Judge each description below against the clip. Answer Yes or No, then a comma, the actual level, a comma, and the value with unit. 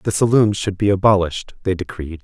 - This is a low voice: Yes, very low, 95 Hz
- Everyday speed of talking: Yes, average, 190 wpm